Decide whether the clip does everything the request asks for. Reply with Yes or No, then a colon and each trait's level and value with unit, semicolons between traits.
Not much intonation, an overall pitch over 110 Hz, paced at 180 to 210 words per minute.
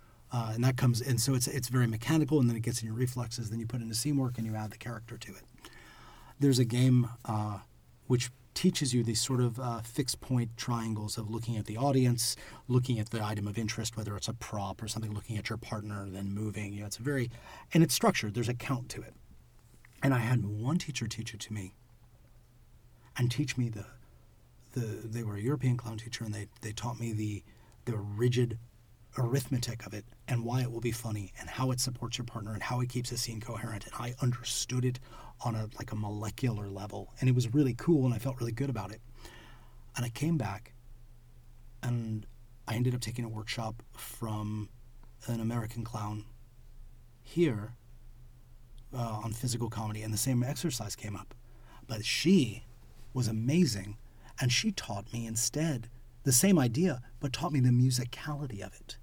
Yes: narrow, 2.1 semitones; low, 120 Hz; average, 200 wpm